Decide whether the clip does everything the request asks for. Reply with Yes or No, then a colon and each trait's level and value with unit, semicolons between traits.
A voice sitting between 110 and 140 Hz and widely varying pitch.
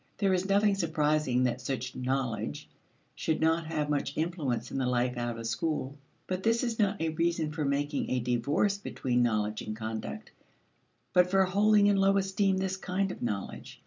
No: medium, 155 Hz; wide, 7.2 semitones